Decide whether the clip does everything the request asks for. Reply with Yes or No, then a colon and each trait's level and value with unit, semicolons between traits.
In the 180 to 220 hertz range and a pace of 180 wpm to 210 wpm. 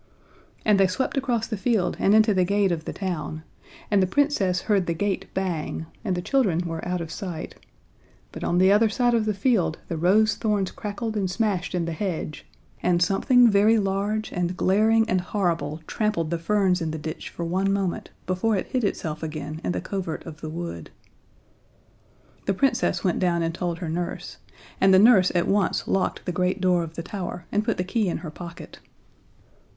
Yes: medium, 185 Hz; average, 200 wpm